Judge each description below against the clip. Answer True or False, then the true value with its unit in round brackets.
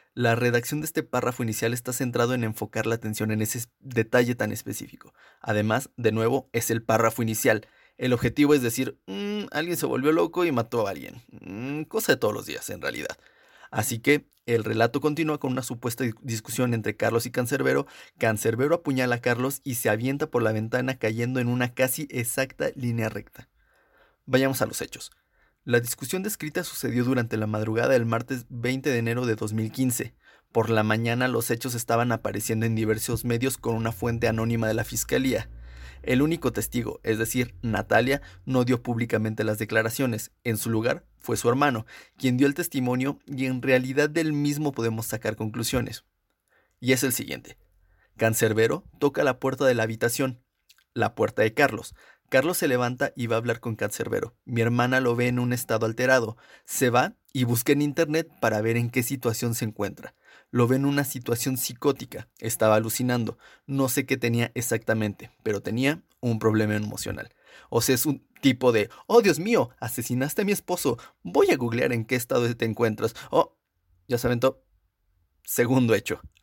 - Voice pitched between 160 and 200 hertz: False (120 Hz)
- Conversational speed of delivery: True (180 wpm)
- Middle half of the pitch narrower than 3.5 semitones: True (2.8 semitones)